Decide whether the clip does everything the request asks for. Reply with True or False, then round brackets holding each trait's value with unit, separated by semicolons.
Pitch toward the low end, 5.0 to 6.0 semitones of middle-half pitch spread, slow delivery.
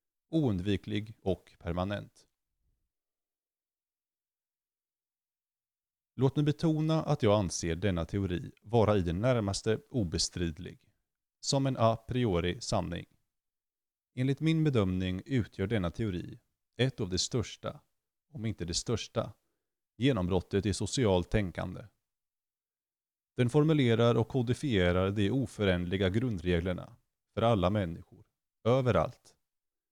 True (105 Hz; 5.3 semitones; 100 wpm)